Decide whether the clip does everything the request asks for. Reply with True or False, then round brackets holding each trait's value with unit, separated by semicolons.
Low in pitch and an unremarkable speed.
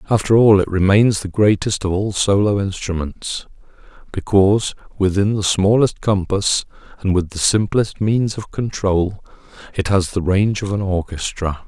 True (100 Hz; 150 wpm)